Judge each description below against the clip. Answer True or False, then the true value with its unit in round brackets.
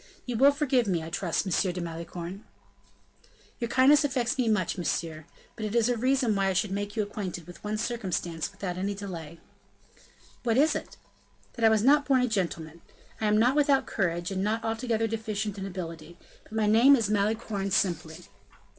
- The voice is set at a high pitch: True (210 Hz)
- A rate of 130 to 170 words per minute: False (190 wpm)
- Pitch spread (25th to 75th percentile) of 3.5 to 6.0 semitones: True (4.7 semitones)